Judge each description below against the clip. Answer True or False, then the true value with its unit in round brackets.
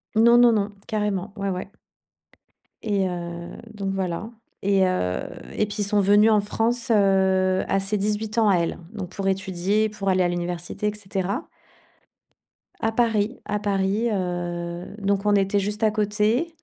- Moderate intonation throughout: False (2.1 semitones)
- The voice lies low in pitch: False (200 Hz)